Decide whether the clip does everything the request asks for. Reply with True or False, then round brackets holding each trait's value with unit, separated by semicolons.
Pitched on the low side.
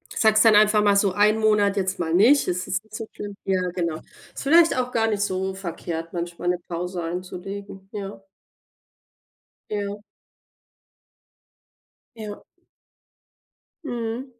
False (200 Hz)